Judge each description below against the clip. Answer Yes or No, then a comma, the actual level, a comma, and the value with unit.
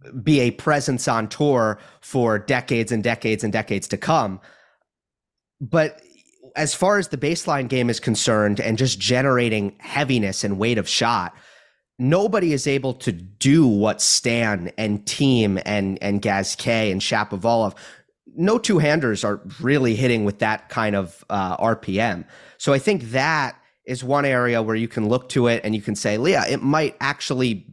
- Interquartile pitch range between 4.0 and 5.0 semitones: Yes, average, 4.4 semitones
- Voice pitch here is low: Yes, low, 120 Hz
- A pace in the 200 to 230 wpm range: No, average, 165 wpm